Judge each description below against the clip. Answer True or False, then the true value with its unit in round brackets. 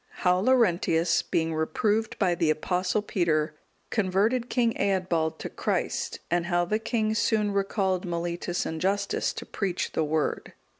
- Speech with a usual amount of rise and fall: True (3.7 semitones)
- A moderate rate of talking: True (145 wpm)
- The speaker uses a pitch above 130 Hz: True (185 Hz)